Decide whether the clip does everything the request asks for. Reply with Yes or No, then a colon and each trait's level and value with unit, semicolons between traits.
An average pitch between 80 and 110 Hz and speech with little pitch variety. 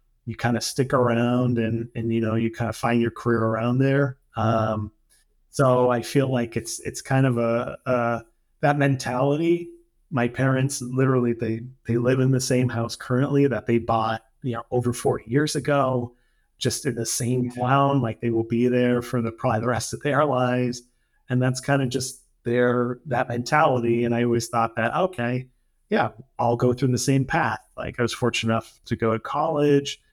No: low, 125 Hz; narrow, 2.3 semitones